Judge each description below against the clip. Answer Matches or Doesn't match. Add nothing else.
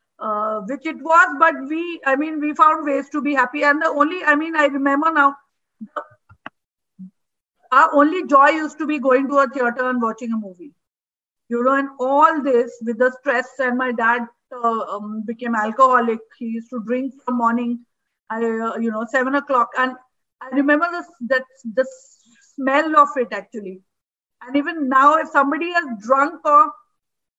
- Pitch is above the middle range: Matches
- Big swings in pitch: Doesn't match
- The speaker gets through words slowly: Doesn't match